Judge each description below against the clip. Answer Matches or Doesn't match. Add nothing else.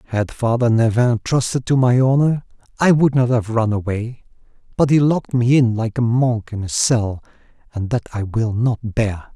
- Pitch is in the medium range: Doesn't match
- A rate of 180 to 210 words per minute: Matches